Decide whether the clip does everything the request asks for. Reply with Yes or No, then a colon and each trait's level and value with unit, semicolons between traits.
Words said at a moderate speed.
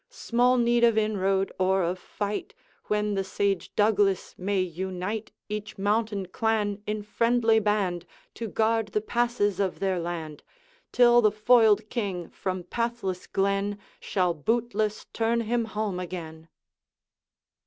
No: slow, 130 wpm